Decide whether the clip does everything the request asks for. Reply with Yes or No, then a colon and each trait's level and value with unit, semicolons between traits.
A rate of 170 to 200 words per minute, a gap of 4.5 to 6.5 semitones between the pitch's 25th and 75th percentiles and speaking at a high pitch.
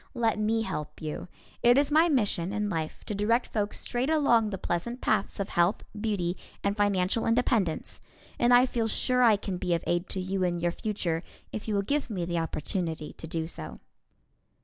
Yes: average, 195 wpm; average, 4.9 semitones; high, 205 Hz